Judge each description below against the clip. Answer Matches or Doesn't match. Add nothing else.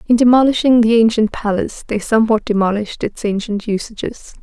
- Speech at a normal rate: Matches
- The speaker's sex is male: Doesn't match